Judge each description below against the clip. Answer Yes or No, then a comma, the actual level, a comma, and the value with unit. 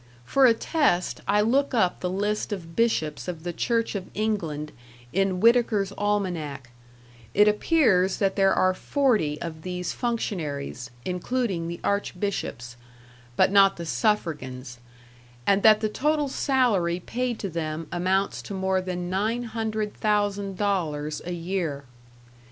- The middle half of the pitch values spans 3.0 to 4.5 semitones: Yes, average, 4.0 semitones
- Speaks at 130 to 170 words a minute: Yes, average, 140 wpm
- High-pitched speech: Yes, high, 195 Hz